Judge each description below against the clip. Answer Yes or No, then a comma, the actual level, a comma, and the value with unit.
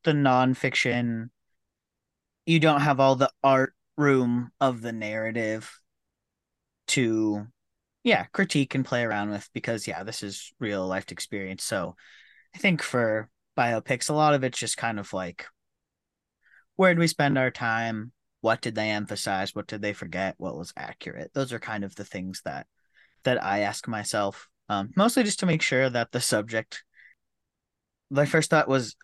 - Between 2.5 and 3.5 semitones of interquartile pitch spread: No, average, 4.5 semitones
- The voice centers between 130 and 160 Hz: No, low, 120 Hz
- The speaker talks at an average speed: Yes, average, 165 wpm